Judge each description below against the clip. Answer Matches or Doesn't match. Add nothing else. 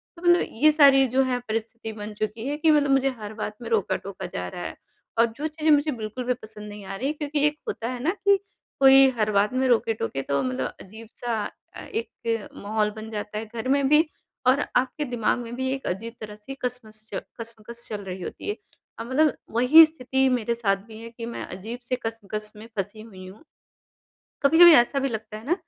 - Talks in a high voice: Matches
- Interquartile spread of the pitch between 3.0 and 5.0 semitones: Matches